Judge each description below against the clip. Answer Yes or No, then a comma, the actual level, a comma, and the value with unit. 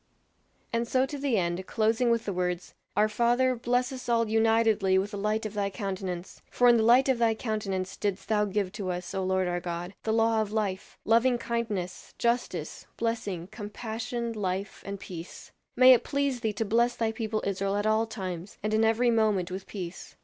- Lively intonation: No, average, 3.4 semitones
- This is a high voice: Yes, high, 215 Hz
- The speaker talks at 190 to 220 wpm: Yes, average, 200 wpm